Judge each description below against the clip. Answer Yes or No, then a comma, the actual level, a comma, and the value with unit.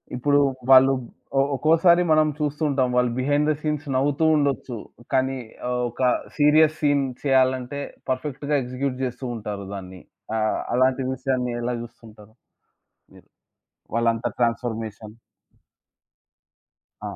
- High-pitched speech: No, low, 130 Hz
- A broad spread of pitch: No, average, 3.3 semitones